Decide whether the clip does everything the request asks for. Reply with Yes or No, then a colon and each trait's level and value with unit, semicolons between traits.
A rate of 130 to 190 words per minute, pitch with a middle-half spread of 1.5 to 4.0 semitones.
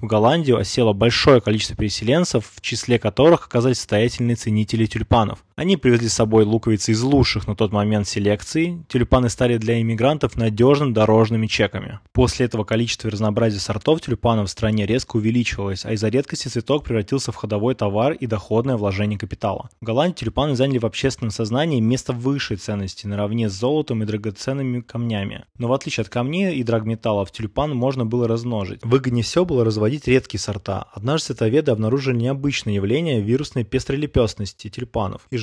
Yes: fast, 160 wpm; average, 3.2 semitones